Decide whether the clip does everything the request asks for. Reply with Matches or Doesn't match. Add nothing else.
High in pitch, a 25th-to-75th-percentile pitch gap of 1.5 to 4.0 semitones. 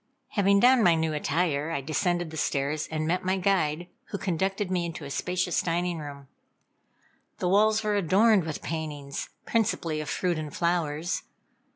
Doesn't match